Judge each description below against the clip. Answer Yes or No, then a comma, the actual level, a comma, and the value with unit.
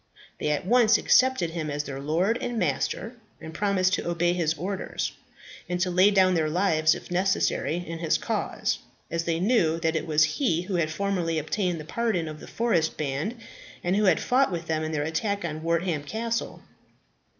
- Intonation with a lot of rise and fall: No, average, 3.9 semitones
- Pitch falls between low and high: Yes, medium, 175 Hz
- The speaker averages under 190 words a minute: No, average, 195 wpm